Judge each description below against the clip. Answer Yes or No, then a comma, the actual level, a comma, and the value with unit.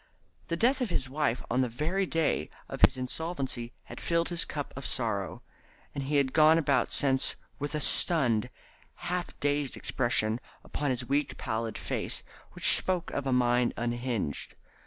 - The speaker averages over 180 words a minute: No, average, 165 wpm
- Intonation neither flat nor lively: Yes, average, 4.5 semitones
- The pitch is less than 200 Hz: Yes, medium, 140 Hz